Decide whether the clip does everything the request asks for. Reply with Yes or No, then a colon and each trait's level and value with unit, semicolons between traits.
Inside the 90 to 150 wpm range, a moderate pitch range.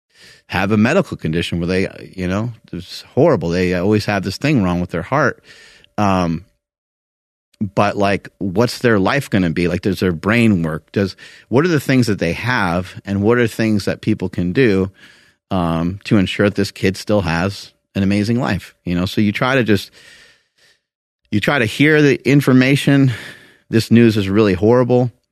No: average, 185 wpm; average, 4.0 semitones